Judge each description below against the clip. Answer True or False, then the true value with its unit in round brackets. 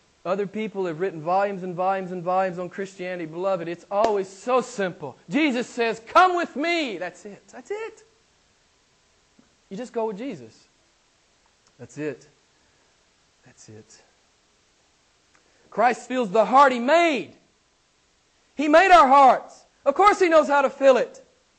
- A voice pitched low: False (225 Hz)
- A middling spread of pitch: False (7.8 semitones)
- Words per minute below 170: True (145 wpm)